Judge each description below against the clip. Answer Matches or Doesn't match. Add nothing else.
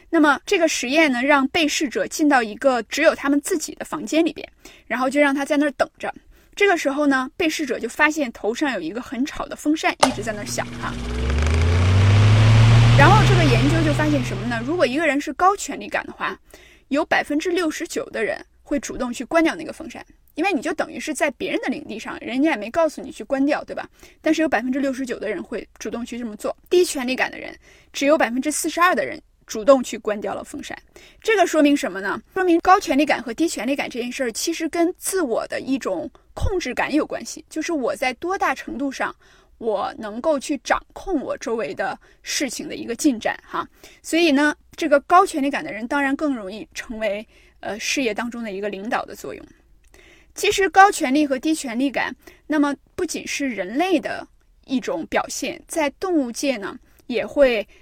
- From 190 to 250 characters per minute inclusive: Doesn't match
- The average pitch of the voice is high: Matches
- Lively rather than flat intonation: Doesn't match